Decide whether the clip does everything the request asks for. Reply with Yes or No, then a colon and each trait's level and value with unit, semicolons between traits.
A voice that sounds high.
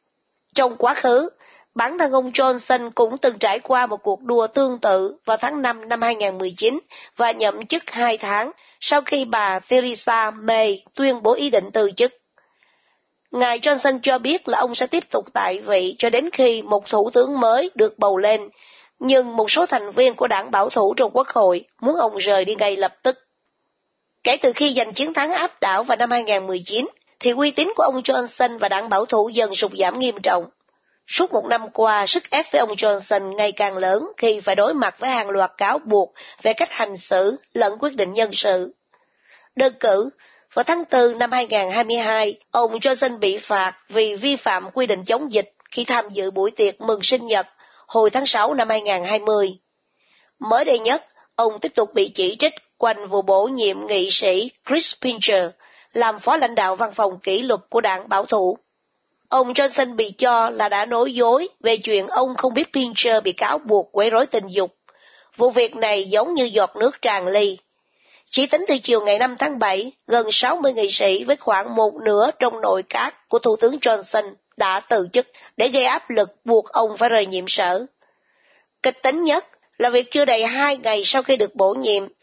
Yes: high, 230 Hz